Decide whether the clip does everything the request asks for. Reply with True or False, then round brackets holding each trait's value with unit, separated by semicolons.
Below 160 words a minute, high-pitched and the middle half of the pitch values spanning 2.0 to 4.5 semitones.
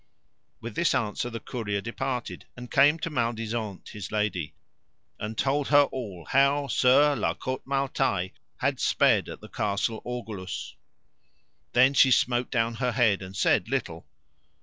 False (150 wpm; 120 Hz; 4.1 semitones)